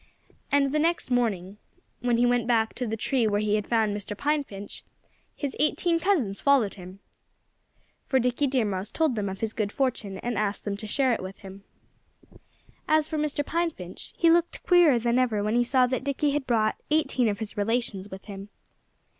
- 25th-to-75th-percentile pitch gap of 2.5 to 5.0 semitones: No, wide, 5.4 semitones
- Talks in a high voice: Yes, high, 235 Hz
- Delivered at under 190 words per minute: No, average, 200 wpm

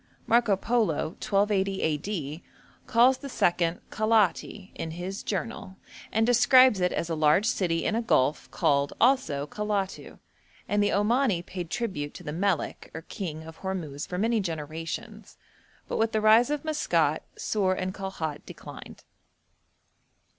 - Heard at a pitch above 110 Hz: Yes, high, 190 Hz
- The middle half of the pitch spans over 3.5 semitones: Yes, average, 5.1 semitones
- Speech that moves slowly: No, average, 145 wpm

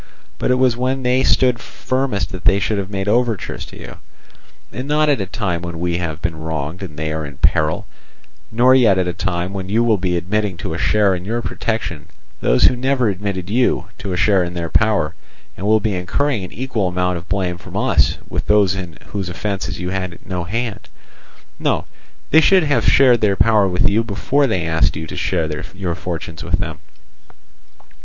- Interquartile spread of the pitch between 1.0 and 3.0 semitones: No, average, 4.6 semitones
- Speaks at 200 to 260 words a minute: Yes, fast, 205 wpm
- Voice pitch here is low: Yes, very low, 95 Hz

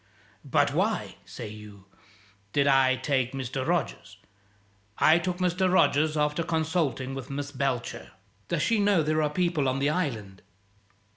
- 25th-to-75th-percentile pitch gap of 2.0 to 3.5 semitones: No, average, 4.2 semitones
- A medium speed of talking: Yes, average, 150 wpm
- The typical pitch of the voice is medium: Yes, medium, 145 Hz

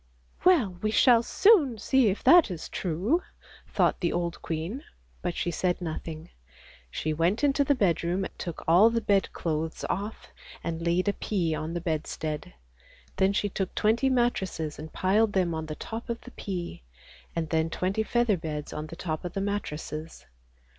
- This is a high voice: No, medium, 180 Hz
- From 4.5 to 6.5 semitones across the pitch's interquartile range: Yes, average, 5.2 semitones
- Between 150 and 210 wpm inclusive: Yes, average, 175 wpm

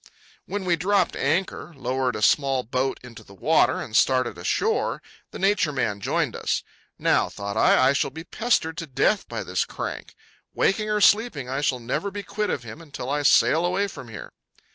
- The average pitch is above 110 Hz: Yes, medium, 140 Hz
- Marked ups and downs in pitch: Yes, wide, 7.2 semitones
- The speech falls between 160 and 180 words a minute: No, average, 190 wpm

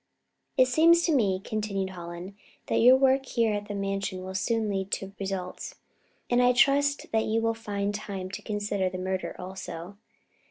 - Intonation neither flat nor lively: Yes, average, 3.5 semitones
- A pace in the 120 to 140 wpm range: No, average, 175 wpm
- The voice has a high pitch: Yes, high, 205 Hz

